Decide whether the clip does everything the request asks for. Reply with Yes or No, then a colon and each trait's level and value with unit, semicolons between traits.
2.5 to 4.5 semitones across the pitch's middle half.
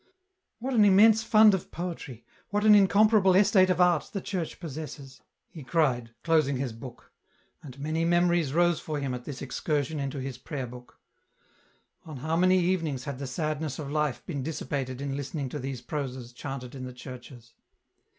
No: average, 4.9 semitones